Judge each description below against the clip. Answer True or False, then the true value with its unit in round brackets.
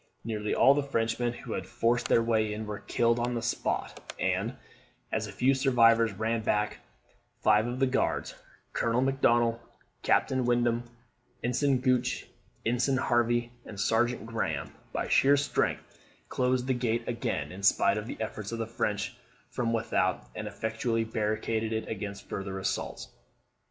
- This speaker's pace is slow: False (155 wpm)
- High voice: False (115 Hz)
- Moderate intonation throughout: False (1.9 semitones)